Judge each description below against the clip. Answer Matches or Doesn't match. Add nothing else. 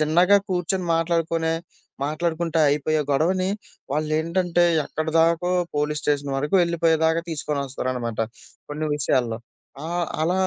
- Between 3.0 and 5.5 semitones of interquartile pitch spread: Doesn't match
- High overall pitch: Doesn't match